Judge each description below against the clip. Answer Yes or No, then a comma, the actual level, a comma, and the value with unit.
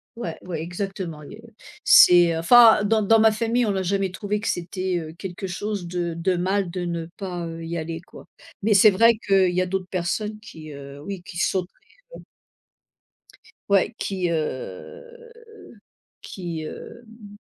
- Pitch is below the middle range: No, medium, 185 Hz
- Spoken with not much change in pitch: No, average, 3.6 semitones